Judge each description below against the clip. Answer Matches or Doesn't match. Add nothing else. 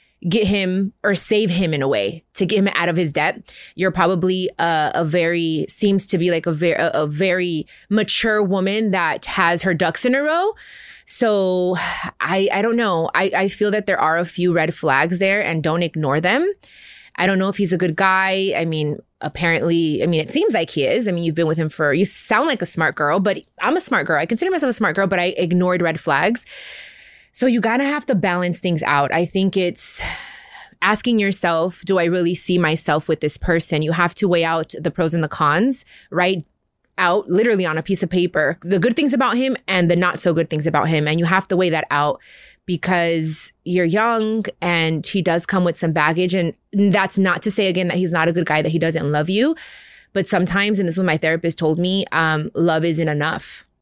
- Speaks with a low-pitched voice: Doesn't match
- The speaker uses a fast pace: Matches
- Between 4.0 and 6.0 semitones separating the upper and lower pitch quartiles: Doesn't match